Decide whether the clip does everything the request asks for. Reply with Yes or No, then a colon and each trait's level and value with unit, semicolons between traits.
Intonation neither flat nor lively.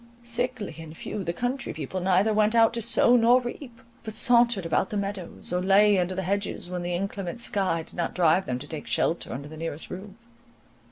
Yes: average, 4.8 semitones